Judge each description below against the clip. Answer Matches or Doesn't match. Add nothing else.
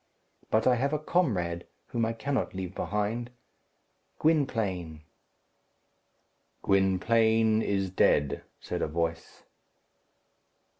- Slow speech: Matches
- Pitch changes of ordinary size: Matches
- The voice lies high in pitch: Doesn't match